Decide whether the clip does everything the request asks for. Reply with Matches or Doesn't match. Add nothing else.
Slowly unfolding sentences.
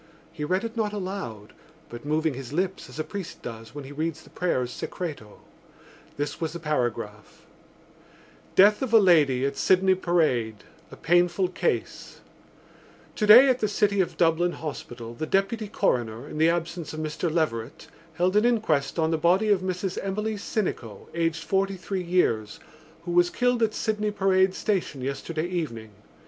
Doesn't match